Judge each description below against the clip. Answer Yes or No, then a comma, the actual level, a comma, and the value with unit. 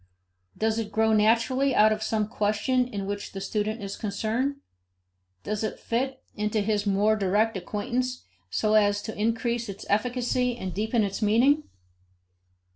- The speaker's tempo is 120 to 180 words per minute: Yes, average, 150 wpm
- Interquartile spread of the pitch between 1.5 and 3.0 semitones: Yes, narrow, 2.4 semitones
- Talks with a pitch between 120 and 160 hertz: No, high, 215 Hz